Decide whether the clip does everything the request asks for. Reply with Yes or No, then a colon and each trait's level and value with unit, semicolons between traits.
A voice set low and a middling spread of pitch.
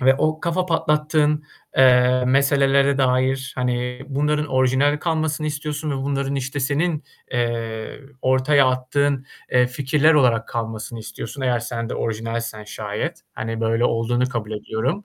Yes: low, 130 Hz; average, 3.5 semitones